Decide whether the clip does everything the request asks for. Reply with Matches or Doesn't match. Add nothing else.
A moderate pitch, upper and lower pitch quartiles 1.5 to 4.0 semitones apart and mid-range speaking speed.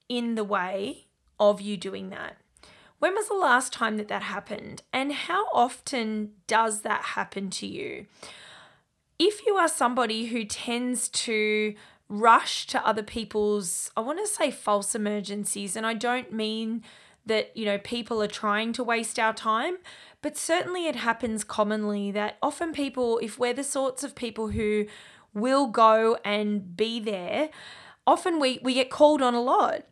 Doesn't match